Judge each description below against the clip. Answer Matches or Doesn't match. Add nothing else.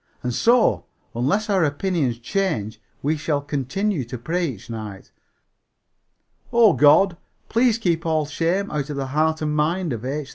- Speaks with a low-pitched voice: Doesn't match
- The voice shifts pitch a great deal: Matches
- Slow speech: Doesn't match